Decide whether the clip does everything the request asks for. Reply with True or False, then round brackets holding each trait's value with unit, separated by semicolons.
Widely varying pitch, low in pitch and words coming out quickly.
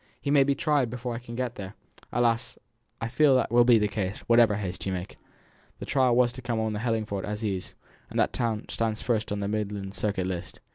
False (3.0 semitones; 115 Hz; 230 wpm)